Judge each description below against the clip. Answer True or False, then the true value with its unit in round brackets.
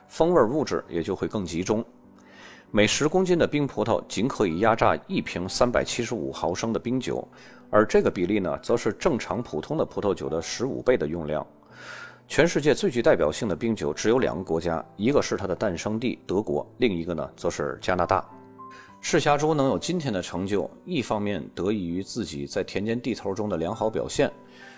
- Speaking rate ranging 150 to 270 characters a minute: False (300 characters per minute)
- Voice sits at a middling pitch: False (105 Hz)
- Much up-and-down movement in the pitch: True (6.7 semitones)